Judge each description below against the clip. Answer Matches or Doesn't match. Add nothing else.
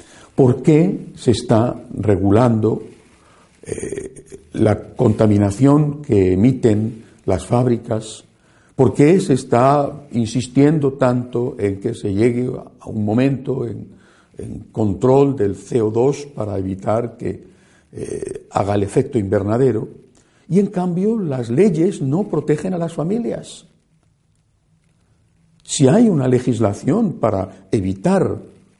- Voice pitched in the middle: Doesn't match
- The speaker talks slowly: Matches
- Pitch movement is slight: Doesn't match